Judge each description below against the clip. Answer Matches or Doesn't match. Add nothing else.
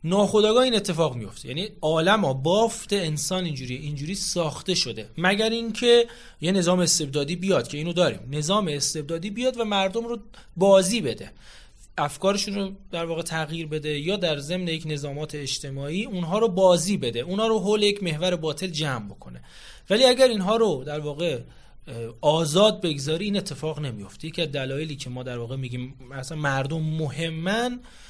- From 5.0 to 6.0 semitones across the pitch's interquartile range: Matches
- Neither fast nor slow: Doesn't match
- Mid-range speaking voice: Matches